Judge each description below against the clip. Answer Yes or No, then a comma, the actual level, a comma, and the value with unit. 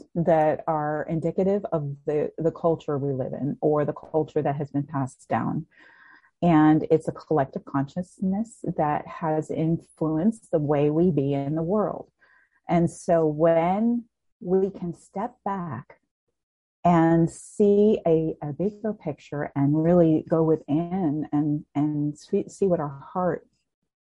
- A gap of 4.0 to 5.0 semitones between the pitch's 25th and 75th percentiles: No, average, 3.3 semitones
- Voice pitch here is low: No, medium, 165 Hz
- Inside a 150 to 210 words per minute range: No, average, 140 wpm